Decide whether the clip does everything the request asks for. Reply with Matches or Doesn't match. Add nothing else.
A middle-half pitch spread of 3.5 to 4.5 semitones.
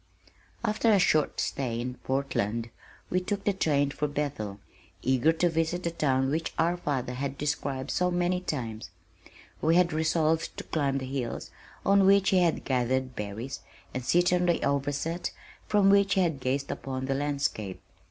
Doesn't match